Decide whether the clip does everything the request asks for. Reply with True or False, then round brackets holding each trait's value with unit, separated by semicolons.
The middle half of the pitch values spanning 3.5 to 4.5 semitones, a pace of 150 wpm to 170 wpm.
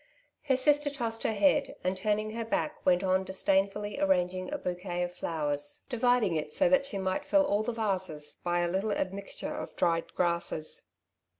False (4.2 semitones; 180 wpm)